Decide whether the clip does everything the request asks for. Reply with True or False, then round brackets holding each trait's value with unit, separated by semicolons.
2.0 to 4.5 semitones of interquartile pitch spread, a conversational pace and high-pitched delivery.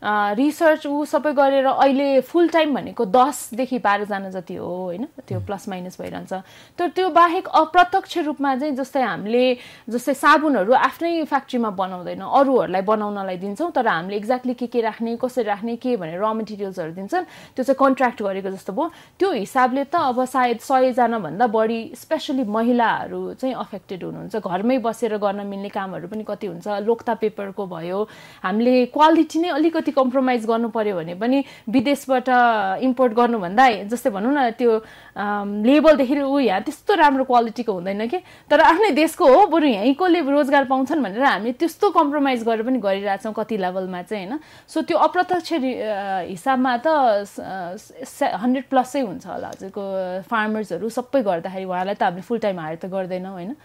False (5.5 semitones; 160 wpm; 245 Hz)